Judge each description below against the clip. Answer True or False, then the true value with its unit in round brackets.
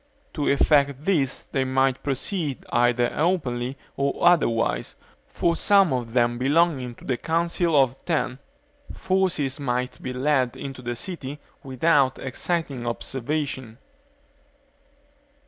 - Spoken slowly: True (115 wpm)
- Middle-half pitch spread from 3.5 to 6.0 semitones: True (4.2 semitones)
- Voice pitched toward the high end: False (135 Hz)